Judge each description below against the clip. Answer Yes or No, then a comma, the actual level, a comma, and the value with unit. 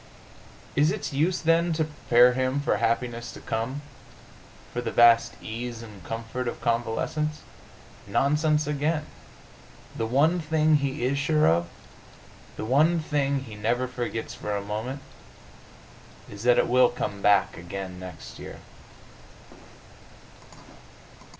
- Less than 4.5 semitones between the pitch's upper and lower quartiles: No, average, 4.8 semitones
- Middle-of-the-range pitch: No, low, 125 Hz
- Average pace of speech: No, slow, 130 wpm